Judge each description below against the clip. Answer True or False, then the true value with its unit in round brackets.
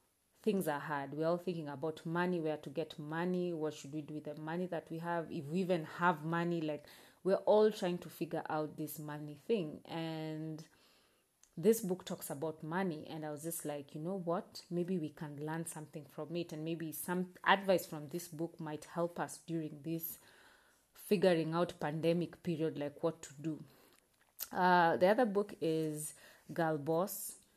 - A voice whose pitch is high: False (165 Hz)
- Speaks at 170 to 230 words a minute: True (185 wpm)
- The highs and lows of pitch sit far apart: False (2.4 semitones)